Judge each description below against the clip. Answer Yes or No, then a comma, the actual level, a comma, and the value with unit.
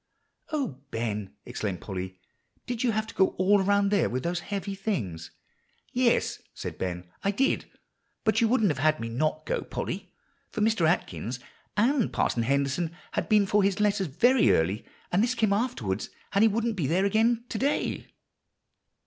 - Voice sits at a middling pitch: No, high, 195 Hz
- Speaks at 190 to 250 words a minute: No, average, 175 wpm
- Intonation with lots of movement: Yes, wide, 8.7 semitones